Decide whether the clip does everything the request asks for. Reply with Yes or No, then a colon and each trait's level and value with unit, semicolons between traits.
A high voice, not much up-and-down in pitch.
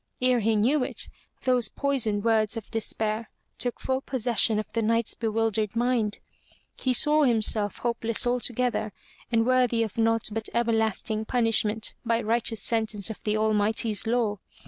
Yes: high, 225 Hz; narrow, 1.9 semitones